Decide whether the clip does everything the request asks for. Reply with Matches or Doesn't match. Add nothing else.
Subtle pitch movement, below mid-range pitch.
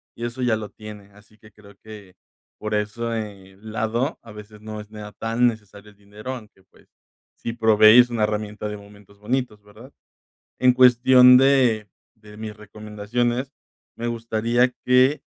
Matches